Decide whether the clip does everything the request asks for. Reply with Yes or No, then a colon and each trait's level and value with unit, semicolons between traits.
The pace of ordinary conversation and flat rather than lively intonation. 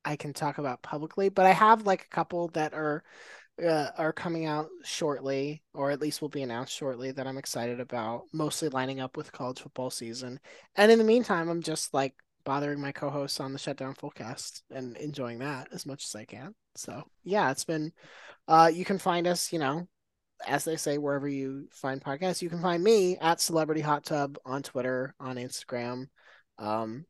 No: average, 195 wpm; average, 3.6 semitones